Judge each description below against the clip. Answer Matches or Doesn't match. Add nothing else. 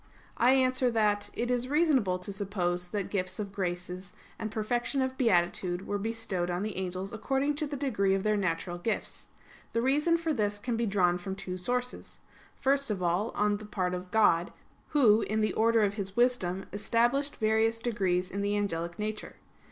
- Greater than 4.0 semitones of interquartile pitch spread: Matches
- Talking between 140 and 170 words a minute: Doesn't match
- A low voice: Doesn't match